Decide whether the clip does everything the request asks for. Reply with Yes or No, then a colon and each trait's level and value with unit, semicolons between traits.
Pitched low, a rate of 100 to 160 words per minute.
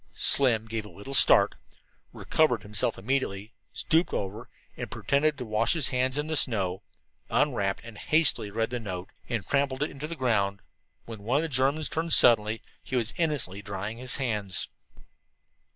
No: low, 120 Hz; average, 170 wpm